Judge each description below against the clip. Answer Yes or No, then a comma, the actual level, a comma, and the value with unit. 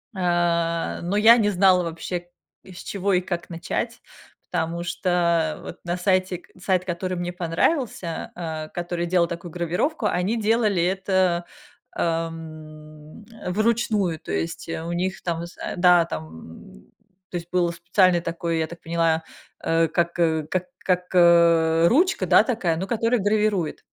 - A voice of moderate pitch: Yes, medium, 175 Hz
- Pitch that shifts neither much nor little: No, narrow, 2.1 semitones